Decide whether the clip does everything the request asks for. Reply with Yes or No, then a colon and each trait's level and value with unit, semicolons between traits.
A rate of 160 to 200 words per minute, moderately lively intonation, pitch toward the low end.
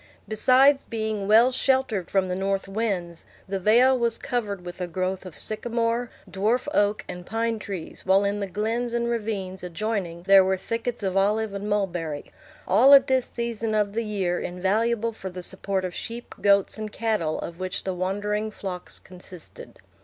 No: average, 175 wpm; average, 3.5 semitones; high, 205 Hz